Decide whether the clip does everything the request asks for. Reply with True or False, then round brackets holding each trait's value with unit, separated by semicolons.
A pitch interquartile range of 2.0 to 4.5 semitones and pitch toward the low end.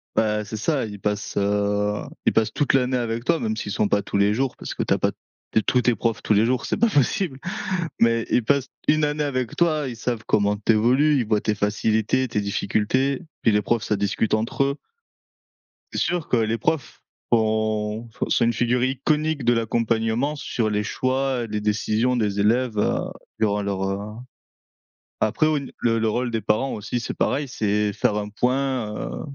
True (3.6 semitones; 115 Hz)